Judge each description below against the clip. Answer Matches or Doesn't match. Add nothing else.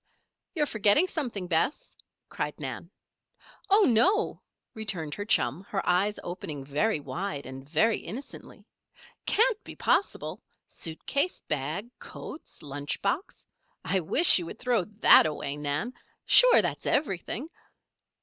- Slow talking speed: Matches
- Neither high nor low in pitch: Doesn't match